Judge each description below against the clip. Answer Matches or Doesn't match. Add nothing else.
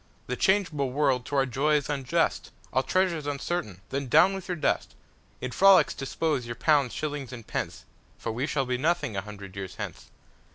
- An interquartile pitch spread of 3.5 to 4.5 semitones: Matches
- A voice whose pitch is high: Doesn't match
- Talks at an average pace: Matches